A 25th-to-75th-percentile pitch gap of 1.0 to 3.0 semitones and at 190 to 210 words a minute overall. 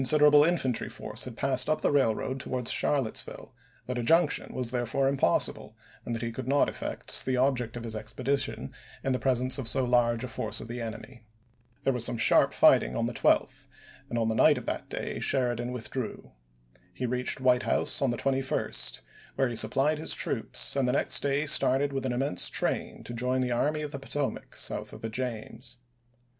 Yes: narrow, 2.4 semitones; average, 200 wpm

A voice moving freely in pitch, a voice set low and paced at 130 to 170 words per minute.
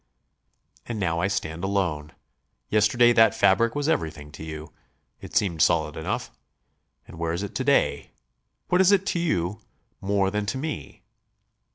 Yes: wide, 5.8 semitones; low, 100 Hz; average, 160 wpm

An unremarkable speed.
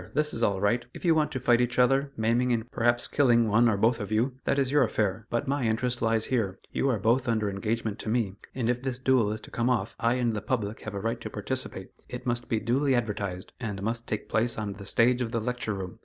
No: fast, 260 wpm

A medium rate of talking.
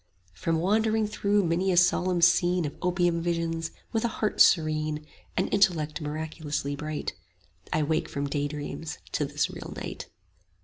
Yes: average, 145 wpm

